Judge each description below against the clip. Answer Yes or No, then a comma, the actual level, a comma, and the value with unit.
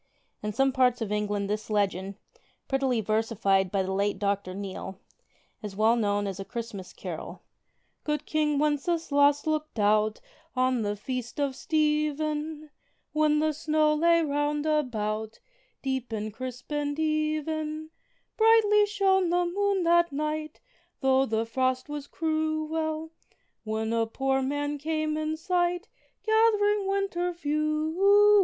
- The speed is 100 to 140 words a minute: Yes, slow, 135 wpm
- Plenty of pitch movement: Yes, wide, 5.9 semitones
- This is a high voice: Yes, very high, 295 Hz